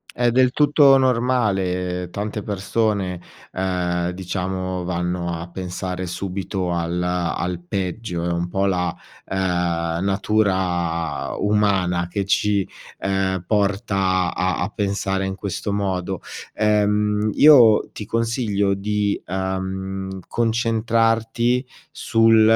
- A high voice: No, very low, 95 Hz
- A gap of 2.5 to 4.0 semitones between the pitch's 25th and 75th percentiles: Yes, average, 2.9 semitones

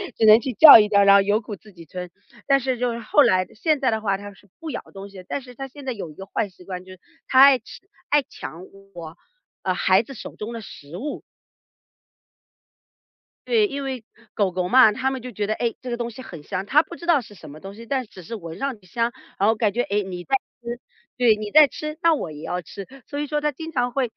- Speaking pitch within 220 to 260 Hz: Yes, high, 225 Hz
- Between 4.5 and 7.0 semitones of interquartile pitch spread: Yes, wide, 5.5 semitones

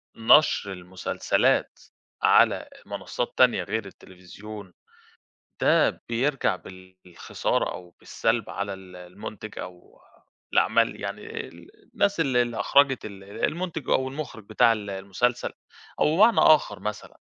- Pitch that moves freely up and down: Yes, wide, 5.8 semitones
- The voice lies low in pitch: Yes, low, 105 Hz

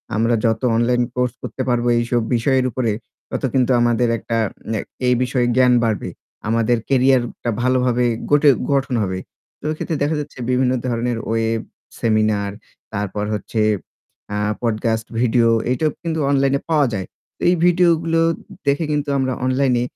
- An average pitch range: Yes, average, 3.0 semitones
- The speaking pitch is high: No, low, 125 Hz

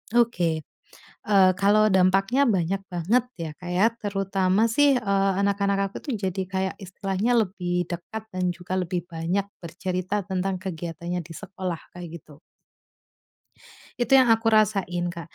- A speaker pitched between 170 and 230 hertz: Yes, high, 190 Hz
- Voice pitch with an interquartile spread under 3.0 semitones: Yes, narrow, 2.5 semitones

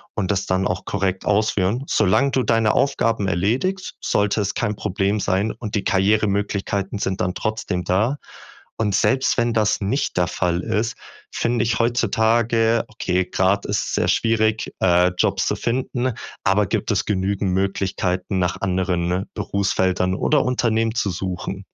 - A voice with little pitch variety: No, average, 3.2 semitones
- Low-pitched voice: Yes, low, 100 Hz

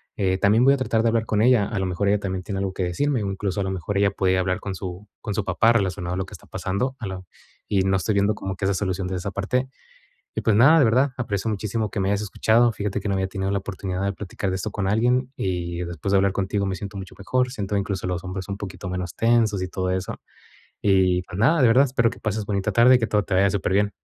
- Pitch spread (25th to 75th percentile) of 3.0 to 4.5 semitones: No, narrow, 2.6 semitones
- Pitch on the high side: No, low, 100 Hz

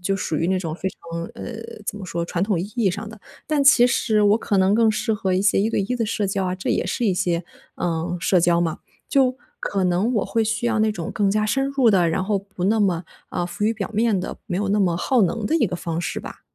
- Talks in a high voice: Yes, high, 200 Hz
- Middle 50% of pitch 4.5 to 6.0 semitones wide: No, average, 3.7 semitones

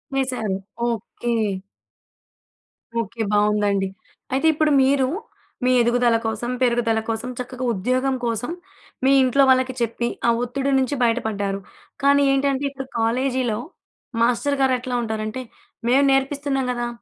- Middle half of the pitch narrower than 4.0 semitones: Yes, average, 2.9 semitones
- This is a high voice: Yes, very high, 250 Hz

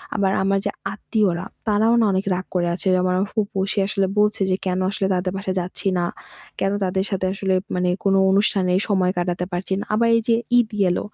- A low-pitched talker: No, high, 190 Hz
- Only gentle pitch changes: Yes, narrow, 2.1 semitones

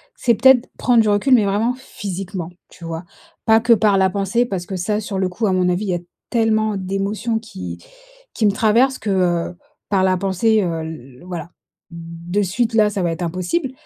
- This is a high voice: Yes, high, 195 Hz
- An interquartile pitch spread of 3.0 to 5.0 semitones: Yes, average, 3.7 semitones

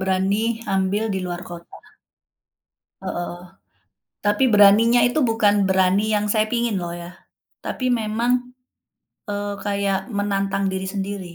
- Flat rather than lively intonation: Yes, narrow, 2.3 semitones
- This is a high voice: Yes, high, 200 Hz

